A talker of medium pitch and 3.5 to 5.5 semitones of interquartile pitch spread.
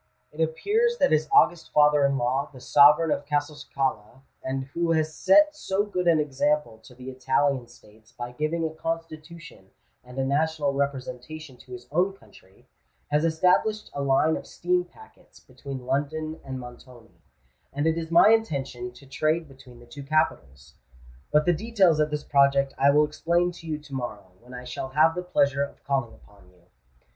Yes: medium, 145 Hz; average, 3.8 semitones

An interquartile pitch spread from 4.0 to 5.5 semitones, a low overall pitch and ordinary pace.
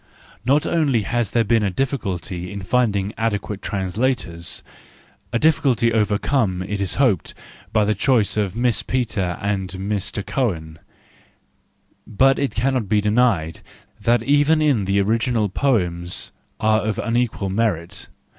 No: average, 4.3 semitones; low, 105 Hz; slow, 130 wpm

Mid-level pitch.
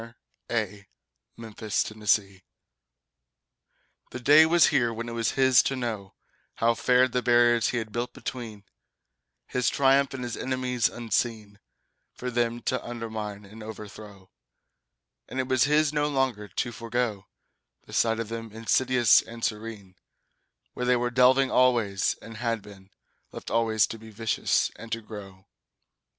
No: low, 115 Hz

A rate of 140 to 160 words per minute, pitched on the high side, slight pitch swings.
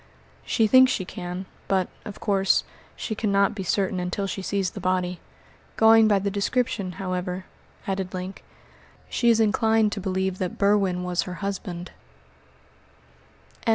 Yes: average, 145 wpm; high, 195 Hz; narrow, 2.2 semitones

